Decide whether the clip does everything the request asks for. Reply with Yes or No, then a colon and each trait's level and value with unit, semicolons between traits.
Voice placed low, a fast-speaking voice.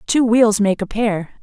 No: high, 215 Hz; fast, 210 wpm